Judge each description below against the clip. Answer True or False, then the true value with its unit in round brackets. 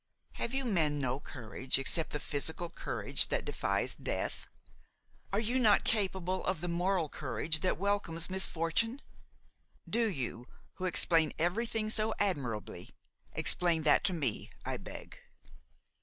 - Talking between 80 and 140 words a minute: True (135 wpm)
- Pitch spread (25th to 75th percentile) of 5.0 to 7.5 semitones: True (5.4 semitones)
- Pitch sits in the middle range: True (175 Hz)